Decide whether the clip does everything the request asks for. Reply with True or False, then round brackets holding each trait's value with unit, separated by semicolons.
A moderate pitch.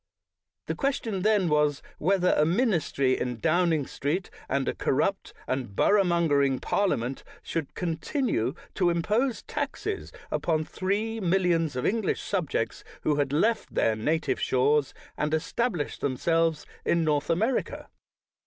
True (165 Hz)